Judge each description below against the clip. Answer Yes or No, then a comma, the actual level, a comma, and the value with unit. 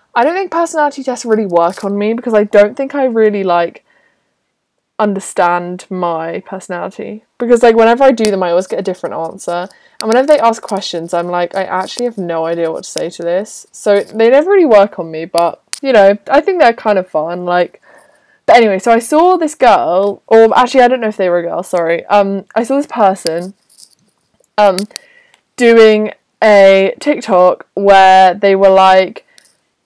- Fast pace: No, average, 195 wpm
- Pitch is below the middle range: No, high, 205 Hz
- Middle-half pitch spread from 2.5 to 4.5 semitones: No, average, 4.9 semitones